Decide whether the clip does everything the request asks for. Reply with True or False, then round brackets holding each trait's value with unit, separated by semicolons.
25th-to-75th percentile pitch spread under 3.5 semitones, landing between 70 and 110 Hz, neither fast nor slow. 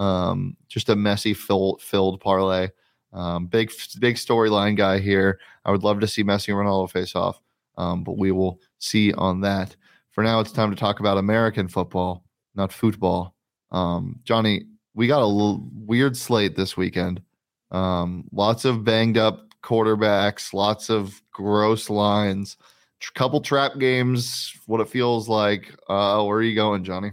True (2.6 semitones; 105 Hz; 165 wpm)